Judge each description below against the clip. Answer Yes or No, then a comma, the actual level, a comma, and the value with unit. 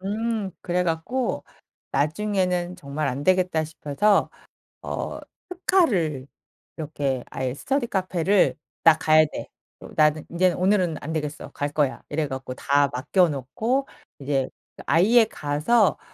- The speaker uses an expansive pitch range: No, average, 5.0 semitones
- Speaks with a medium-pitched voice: Yes, medium, 165 Hz